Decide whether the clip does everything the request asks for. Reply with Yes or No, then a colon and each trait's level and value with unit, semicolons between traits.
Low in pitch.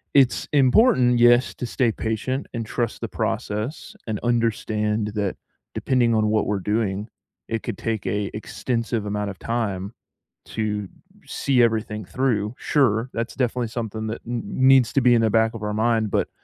Yes: low, 115 Hz